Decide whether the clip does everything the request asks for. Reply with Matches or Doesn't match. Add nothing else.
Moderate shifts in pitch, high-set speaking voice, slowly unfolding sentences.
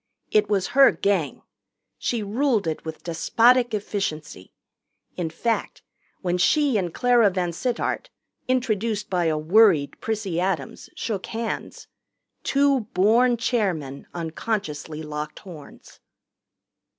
Doesn't match